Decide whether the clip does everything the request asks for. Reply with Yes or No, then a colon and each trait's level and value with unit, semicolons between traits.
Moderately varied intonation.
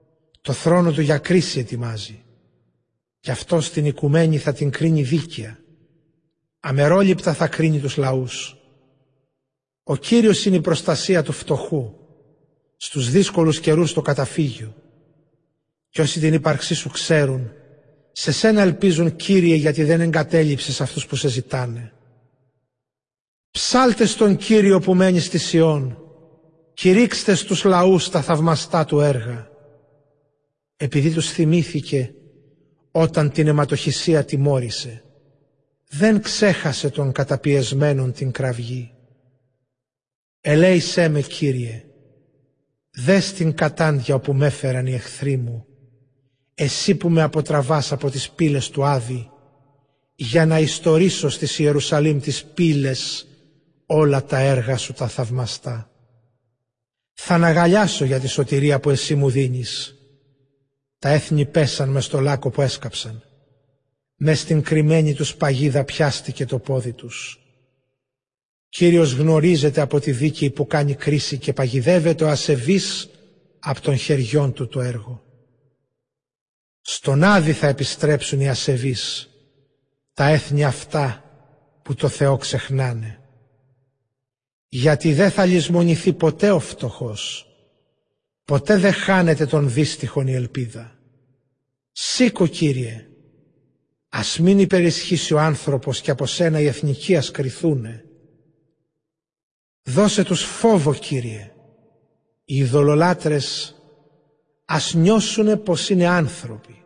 Yes: average, 3.3 semitones